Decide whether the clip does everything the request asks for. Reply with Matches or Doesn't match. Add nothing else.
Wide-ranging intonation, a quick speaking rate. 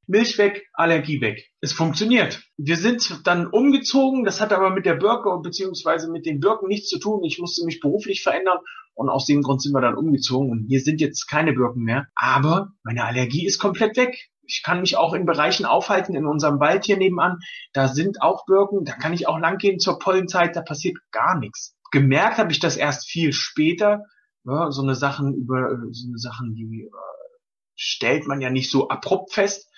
Matches